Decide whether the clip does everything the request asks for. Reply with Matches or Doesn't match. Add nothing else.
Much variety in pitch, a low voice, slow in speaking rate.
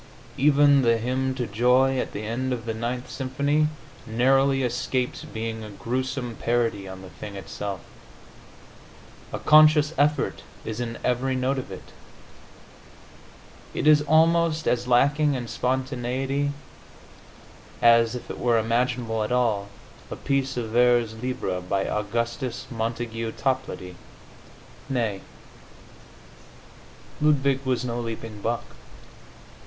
Doesn't match